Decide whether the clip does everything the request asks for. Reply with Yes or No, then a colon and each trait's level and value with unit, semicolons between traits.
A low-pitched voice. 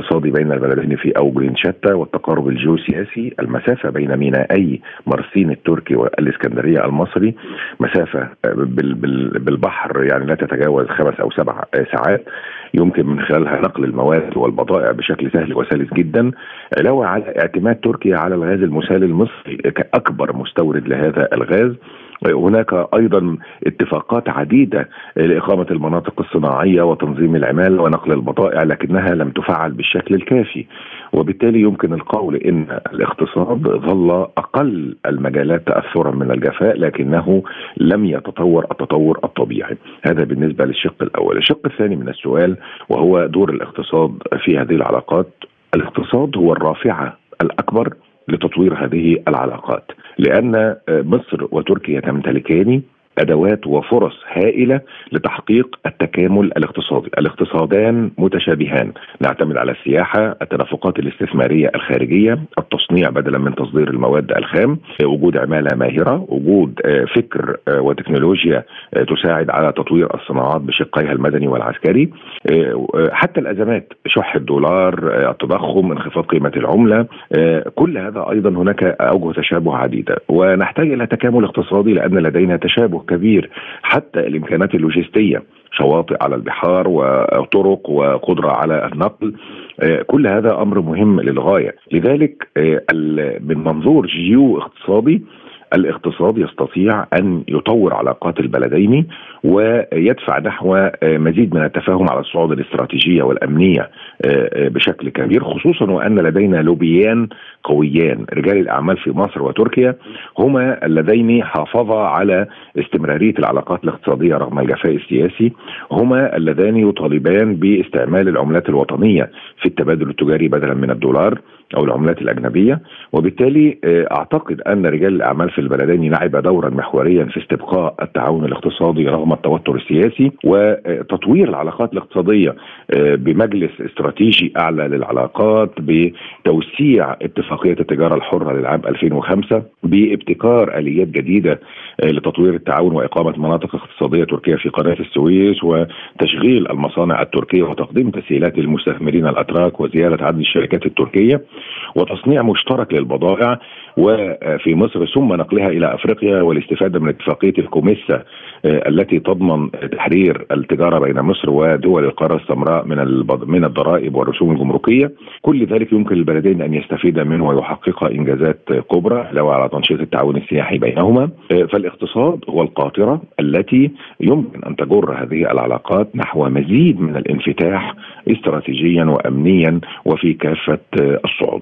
Yes: very low, 85 Hz